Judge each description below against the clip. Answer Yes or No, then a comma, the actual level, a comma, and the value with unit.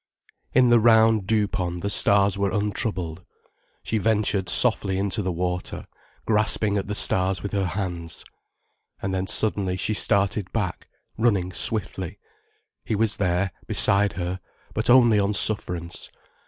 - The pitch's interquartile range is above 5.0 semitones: No, narrow, 2.6 semitones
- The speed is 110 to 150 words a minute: Yes, average, 140 wpm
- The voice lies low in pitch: Yes, low, 100 Hz